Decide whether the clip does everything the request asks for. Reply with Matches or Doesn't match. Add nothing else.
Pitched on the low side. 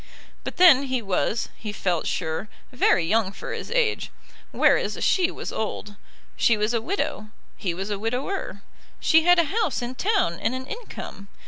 Doesn't match